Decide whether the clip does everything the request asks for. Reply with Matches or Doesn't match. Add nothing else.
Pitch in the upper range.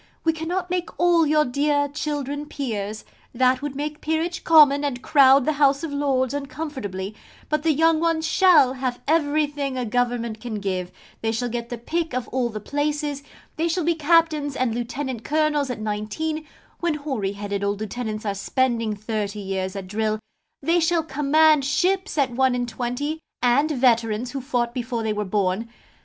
Matches